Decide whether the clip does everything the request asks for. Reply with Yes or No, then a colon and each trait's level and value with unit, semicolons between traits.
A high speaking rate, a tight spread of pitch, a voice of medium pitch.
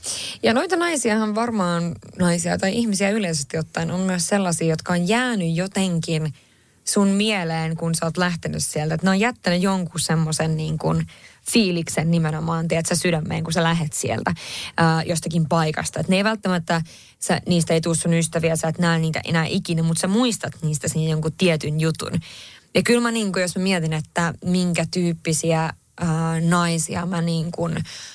Yes: fast, 175 wpm; narrow, 2.1 semitones; medium, 170 Hz